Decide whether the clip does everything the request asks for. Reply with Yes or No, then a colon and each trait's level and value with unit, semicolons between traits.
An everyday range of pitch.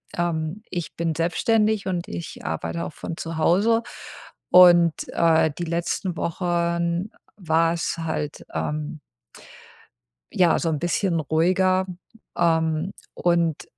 No: narrow, 1.9 semitones